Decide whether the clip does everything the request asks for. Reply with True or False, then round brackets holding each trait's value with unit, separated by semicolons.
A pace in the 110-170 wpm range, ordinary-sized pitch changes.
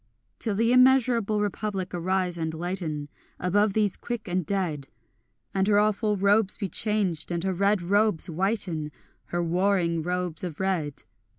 True (150 wpm; 3.3 semitones)